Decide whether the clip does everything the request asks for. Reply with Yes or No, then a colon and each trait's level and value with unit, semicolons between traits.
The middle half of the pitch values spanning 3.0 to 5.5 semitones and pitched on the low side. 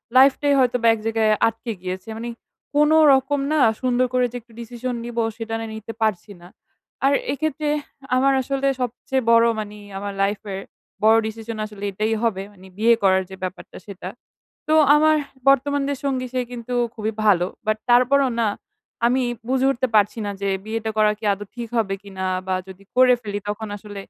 No: average, 3.7 semitones; high, 225 Hz